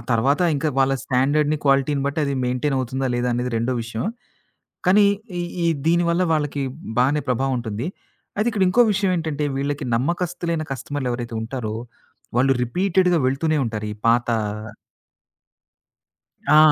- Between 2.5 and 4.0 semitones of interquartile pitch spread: No, average, 4.4 semitones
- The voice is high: No, medium, 140 Hz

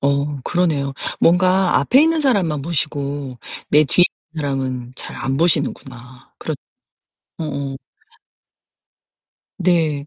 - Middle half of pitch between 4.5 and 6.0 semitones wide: No, average, 4.0 semitones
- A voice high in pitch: No, medium, 145 Hz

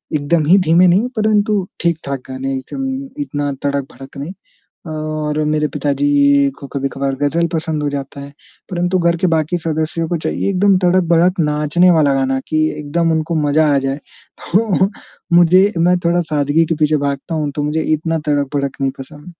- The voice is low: No, medium, 155 Hz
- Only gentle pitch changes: No, average, 3.5 semitones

